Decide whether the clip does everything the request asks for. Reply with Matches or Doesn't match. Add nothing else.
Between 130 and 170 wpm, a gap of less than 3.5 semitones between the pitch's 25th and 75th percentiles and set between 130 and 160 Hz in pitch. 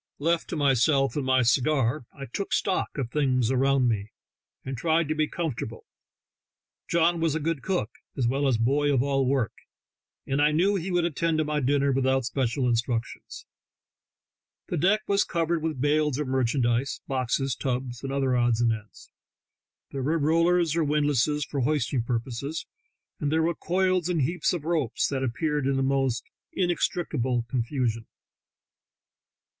Doesn't match